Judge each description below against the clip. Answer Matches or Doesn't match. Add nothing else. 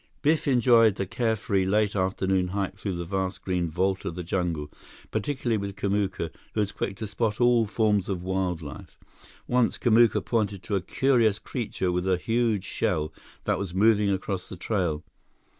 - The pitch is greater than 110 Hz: Doesn't match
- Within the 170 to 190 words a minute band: Matches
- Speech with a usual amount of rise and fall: Matches